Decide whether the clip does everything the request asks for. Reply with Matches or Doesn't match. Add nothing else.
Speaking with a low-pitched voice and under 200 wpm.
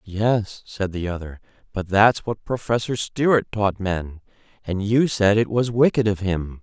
Matches